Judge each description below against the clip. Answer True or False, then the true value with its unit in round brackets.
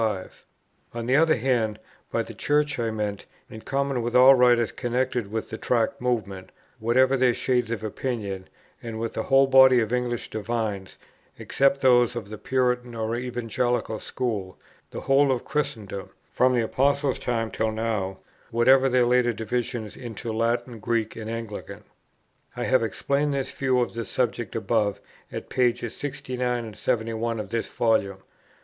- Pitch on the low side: True (120 Hz)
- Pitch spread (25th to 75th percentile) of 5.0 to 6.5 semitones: False (2.5 semitones)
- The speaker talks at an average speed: True (155 wpm)